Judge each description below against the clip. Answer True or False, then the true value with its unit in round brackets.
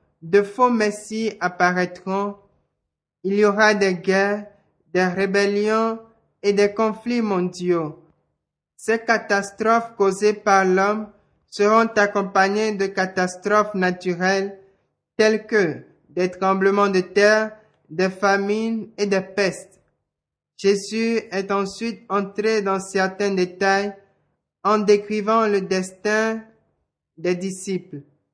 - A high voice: True (200 Hz)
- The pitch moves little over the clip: True (2.1 semitones)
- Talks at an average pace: False (105 wpm)